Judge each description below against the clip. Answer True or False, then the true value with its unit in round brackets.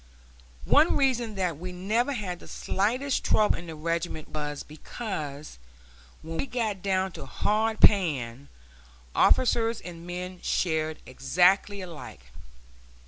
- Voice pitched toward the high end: False (180 Hz)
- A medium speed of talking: False (125 wpm)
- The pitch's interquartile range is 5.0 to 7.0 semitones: True (5.3 semitones)